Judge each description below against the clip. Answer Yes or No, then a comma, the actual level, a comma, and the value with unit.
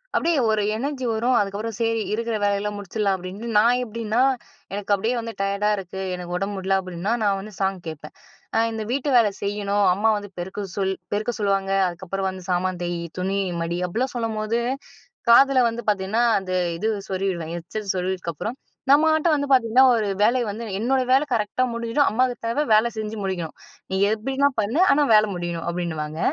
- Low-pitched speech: No, high, 210 Hz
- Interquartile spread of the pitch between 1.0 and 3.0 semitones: No, average, 3.5 semitones